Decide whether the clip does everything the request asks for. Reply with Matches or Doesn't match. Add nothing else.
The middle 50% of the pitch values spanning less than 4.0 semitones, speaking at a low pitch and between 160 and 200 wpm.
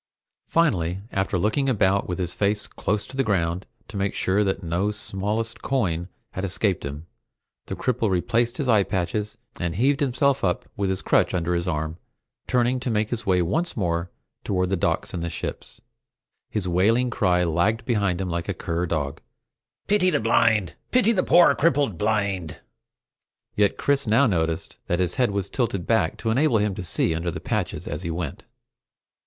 Doesn't match